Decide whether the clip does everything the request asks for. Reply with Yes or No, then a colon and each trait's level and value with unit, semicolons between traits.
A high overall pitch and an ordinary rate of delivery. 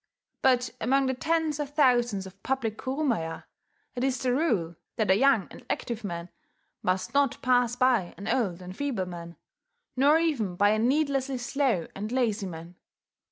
Yes: high, 245 Hz; average, 165 wpm